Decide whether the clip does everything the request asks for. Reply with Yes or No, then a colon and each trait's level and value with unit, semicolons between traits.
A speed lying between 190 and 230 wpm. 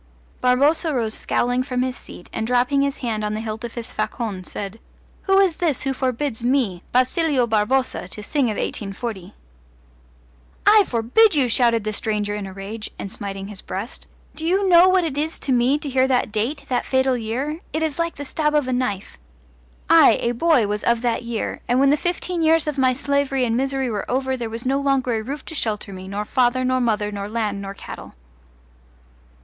Yes: fast, 205 wpm